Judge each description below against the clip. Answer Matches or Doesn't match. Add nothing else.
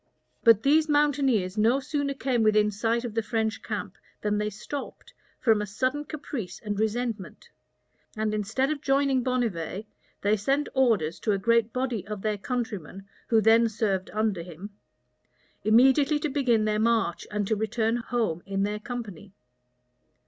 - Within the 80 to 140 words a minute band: Doesn't match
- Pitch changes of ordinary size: Matches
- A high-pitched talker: Matches